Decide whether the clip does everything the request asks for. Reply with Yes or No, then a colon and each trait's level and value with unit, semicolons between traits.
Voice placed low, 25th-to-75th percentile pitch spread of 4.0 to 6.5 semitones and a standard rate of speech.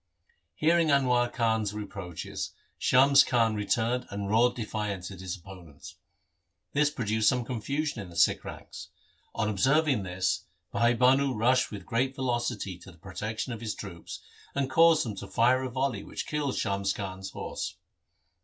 Yes: low, 115 Hz; average, 4.8 semitones; average, 155 wpm